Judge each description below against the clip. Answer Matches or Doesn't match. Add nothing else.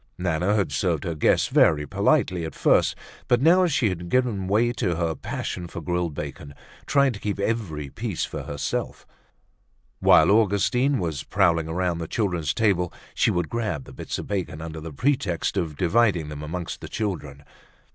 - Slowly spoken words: Doesn't match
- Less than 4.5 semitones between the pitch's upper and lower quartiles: Doesn't match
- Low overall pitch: Matches